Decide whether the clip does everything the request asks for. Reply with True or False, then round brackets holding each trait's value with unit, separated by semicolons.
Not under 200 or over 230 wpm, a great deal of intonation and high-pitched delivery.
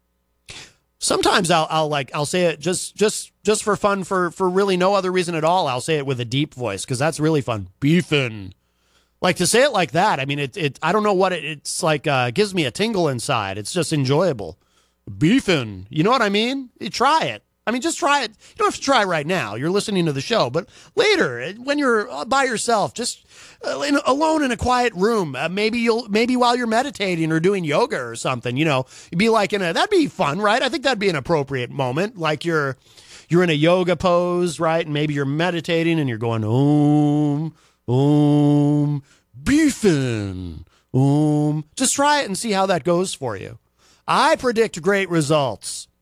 False (205 wpm; 6.3 semitones; 170 Hz)